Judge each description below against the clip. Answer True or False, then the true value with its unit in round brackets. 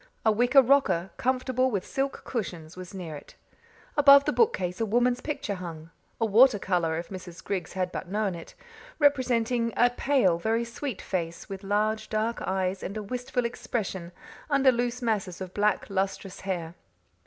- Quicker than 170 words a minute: False (165 wpm)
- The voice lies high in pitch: True (210 Hz)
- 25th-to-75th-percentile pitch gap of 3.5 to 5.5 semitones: True (5.0 semitones)